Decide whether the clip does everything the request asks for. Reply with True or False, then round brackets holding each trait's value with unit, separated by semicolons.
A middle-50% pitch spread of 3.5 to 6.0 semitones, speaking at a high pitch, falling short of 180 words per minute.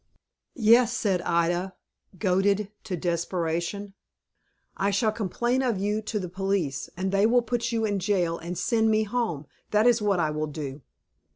True (4.1 semitones; 195 Hz; 165 wpm)